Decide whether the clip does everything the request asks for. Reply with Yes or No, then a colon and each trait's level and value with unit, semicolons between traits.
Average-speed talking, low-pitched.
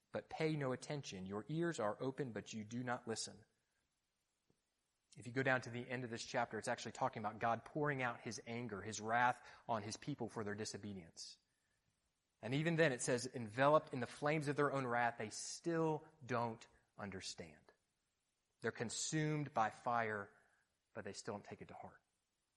Yes: average, 185 wpm; low, 120 Hz